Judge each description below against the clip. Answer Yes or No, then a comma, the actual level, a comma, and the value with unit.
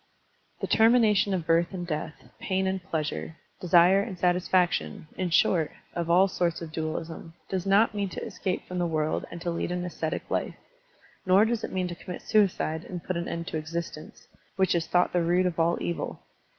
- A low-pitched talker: No, medium, 175 Hz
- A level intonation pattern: Yes, narrow, 2.2 semitones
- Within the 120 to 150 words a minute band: No, average, 195 wpm